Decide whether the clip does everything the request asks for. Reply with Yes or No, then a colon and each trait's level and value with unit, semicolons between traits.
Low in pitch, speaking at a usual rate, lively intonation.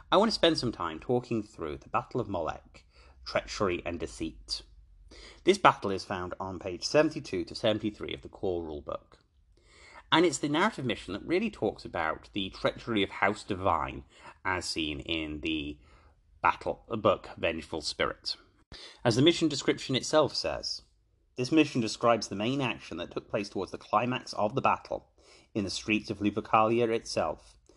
Yes: low, 105 Hz; average, 170 wpm; wide, 7.5 semitones